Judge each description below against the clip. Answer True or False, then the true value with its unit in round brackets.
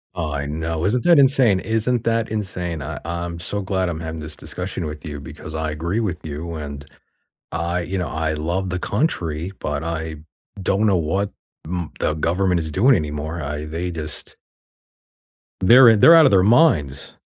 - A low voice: True (85 Hz)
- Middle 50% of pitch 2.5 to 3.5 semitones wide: False (4.1 semitones)